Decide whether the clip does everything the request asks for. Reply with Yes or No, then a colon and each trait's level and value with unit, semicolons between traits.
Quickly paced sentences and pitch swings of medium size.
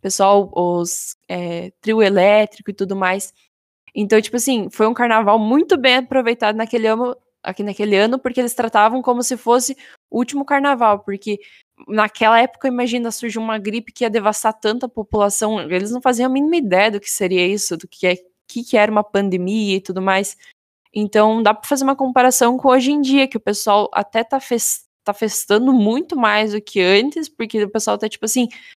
Yes: fast, 195 wpm; average, 3.4 semitones